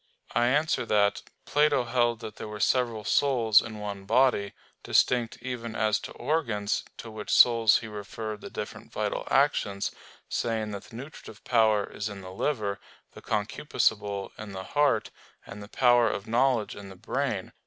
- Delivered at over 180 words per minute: No, average, 165 wpm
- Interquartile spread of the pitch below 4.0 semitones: Yes, average, 3.1 semitones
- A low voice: Yes, low, 110 Hz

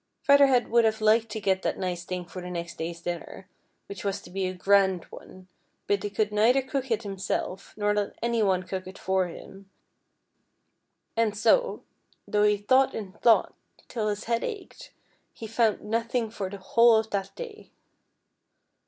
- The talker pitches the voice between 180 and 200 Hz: No, high, 210 Hz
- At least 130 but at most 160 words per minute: No, average, 190 wpm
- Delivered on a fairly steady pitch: No, average, 3.3 semitones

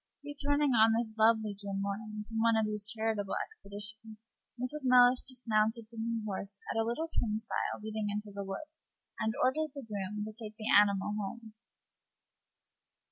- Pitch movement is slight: Yes, narrow, 2.1 semitones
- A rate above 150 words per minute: Yes, average, 160 wpm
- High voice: Yes, high, 220 Hz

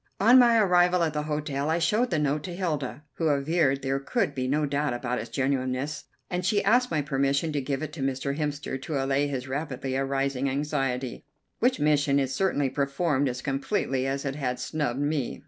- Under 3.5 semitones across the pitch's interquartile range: Yes, average, 2.8 semitones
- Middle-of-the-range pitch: Yes, medium, 145 Hz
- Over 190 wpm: Yes, average, 200 wpm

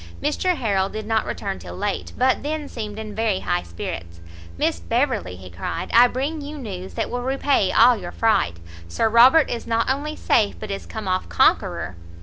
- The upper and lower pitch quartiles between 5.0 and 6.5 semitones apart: Yes, wide, 5.5 semitones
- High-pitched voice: Yes, high, 220 Hz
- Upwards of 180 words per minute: Yes, average, 190 wpm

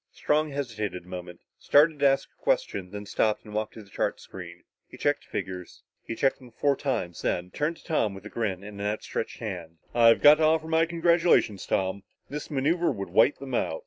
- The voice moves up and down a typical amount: No, wide, 7.3 semitones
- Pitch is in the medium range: No, low, 115 Hz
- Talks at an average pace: No, fast, 215 wpm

